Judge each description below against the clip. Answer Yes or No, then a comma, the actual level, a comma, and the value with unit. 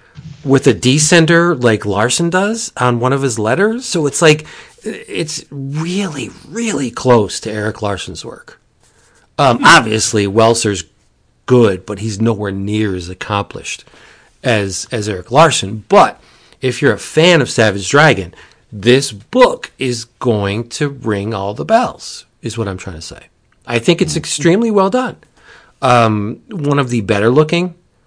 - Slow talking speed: No, average, 150 wpm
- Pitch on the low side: Yes, low, 120 Hz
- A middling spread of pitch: No, wide, 6.6 semitones